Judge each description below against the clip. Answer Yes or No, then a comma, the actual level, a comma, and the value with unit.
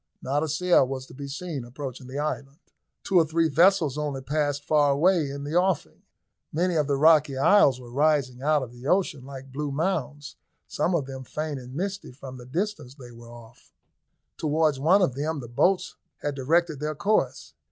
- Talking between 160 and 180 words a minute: No, average, 190 wpm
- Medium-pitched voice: Yes, medium, 145 Hz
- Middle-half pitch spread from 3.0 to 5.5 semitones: Yes, average, 3.3 semitones